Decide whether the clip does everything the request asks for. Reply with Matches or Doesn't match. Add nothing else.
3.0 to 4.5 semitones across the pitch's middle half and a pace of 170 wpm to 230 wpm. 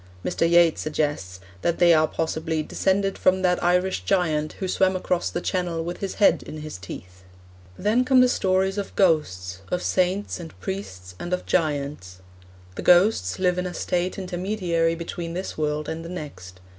Matches